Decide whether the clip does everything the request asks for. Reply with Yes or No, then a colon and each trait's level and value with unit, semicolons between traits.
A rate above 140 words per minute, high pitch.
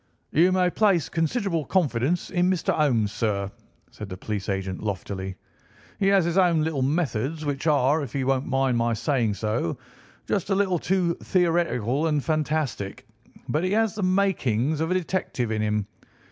No: average, 170 wpm; medium, 150 Hz